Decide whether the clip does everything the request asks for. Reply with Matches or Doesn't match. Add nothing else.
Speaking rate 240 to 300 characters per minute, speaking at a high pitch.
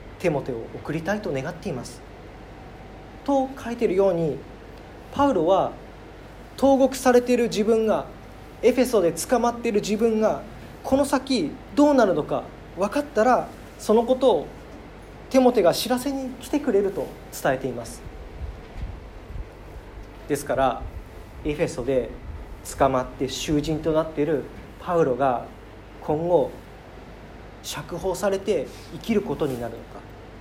Matches